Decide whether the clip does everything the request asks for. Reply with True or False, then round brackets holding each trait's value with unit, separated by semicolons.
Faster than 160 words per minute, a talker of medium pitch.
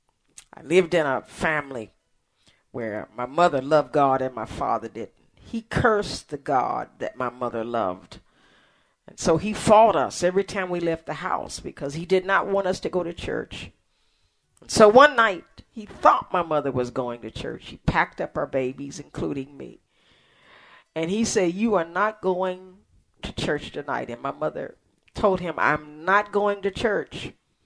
True (180 wpm; 180 Hz)